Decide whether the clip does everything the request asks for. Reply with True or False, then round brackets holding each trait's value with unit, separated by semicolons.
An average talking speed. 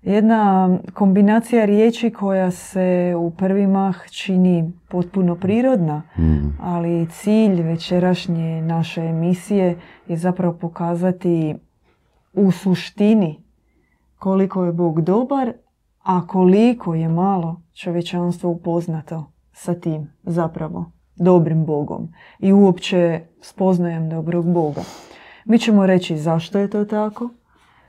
False (105 wpm)